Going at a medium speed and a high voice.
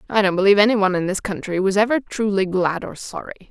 No: fast, 240 wpm; high, 200 Hz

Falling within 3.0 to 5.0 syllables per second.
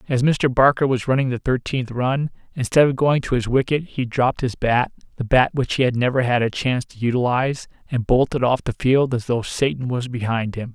No: 5.5 syllables/s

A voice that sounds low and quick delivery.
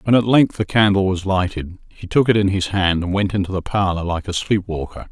Yes: very low, 95 Hz; fast, 245 wpm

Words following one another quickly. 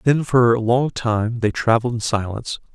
No: average, 195 wpm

